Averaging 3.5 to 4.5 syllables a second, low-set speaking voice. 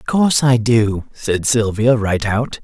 Yes: 4.0 syllables/s; low, 115 Hz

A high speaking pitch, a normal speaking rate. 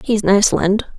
Yes: high, 200 Hz; average, 185 wpm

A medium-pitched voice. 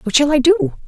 No: very high, 255 Hz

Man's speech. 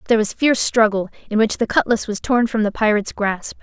No: female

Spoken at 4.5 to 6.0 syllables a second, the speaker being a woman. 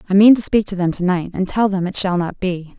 Yes: 5.9 syllables/s; female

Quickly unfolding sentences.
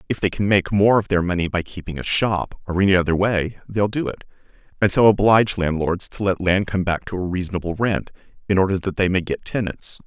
Yes: fast, 230 wpm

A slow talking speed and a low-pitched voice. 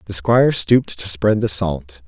No: average, 200 wpm; very low, 95 Hz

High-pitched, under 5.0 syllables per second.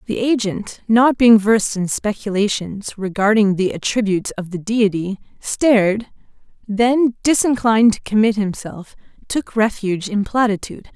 Yes: high, 215 Hz; 4.7 syllables/s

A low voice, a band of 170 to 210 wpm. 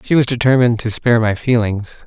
Yes: low, 115 Hz; fast, 205 wpm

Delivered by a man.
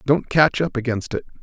Yes: male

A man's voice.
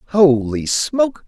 Yes: male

